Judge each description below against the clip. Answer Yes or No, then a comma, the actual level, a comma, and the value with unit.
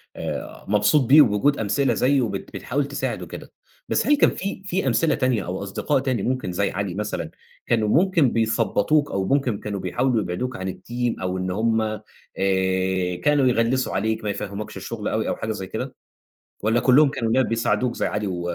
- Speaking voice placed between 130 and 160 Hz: No, low, 115 Hz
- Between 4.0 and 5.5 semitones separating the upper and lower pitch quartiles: Yes, average, 4.5 semitones